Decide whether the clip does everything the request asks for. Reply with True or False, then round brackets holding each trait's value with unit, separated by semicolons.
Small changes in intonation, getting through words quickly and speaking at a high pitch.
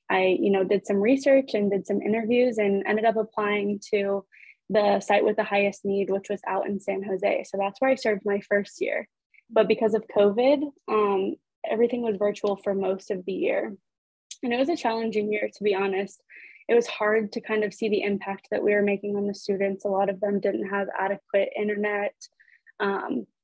True (1.8 semitones; 210 wpm; 205 Hz)